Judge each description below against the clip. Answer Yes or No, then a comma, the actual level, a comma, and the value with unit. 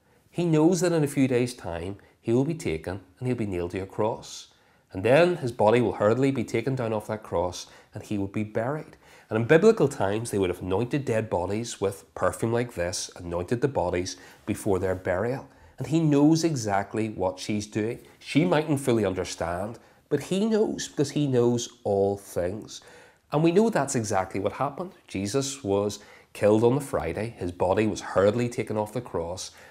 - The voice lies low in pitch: Yes, low, 110 Hz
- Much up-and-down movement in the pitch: Yes, wide, 5.9 semitones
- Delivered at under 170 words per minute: No, average, 195 wpm